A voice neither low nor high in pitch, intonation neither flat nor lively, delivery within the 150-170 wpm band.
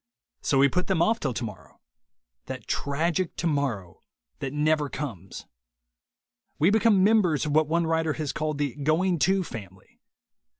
Yes: medium, 150 Hz; average, 4.2 semitones; average, 155 wpm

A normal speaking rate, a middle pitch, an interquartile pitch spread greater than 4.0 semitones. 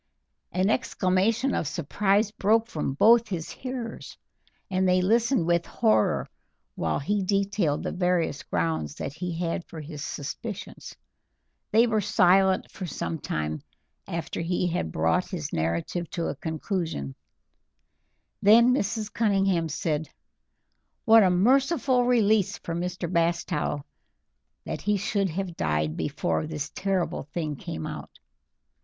No: slow, 130 wpm; medium, 180 Hz; average, 5.0 semitones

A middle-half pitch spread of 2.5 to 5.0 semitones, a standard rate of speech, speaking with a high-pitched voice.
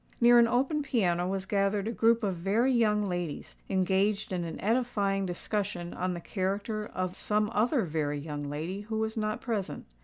Yes: average, 3.5 semitones; average, 180 wpm; high, 200 Hz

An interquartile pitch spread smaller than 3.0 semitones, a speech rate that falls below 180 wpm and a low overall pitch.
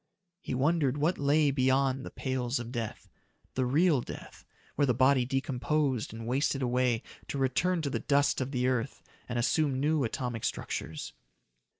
Yes: narrow, 2.4 semitones; average, 165 wpm; low, 130 Hz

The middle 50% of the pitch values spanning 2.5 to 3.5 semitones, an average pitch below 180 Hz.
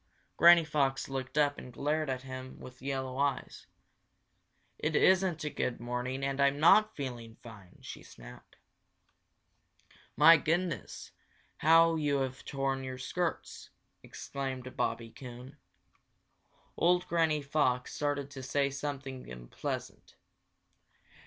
Yes: average, 2.9 semitones; low, 135 Hz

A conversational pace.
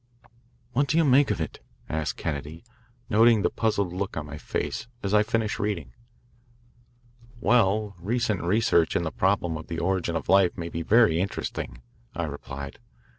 Yes: average, 165 wpm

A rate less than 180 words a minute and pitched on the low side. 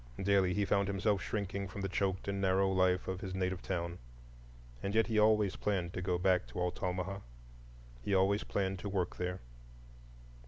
Yes: average, 165 wpm; very low, 95 Hz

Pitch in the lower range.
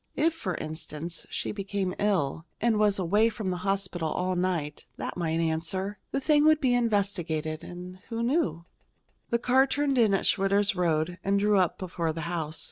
No: high, 190 Hz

